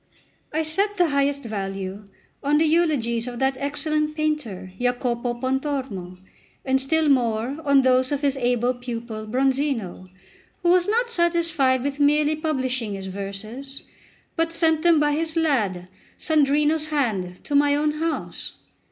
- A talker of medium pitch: No, very high, 275 Hz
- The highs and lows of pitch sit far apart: No, average, 4.5 semitones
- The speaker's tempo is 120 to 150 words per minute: Yes, average, 145 wpm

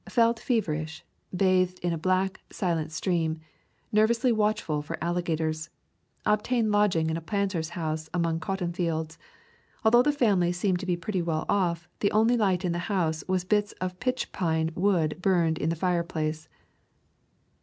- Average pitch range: Yes, average, 4.0 semitones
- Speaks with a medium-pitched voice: Yes, medium, 180 Hz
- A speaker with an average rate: Yes, average, 160 wpm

